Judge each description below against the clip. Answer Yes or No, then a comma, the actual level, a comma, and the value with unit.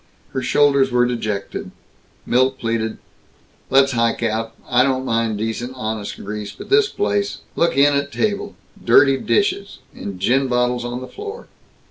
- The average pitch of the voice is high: No, low, 125 Hz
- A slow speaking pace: No, average, 150 wpm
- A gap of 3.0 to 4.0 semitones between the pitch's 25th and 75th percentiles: Yes, average, 3.5 semitones